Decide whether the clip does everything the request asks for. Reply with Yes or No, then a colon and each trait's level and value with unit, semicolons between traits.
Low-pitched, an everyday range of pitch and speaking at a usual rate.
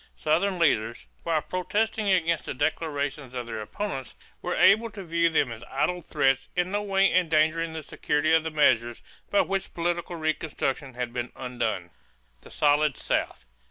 No: medium, 155 Hz; average, 4.9 semitones; average, 160 wpm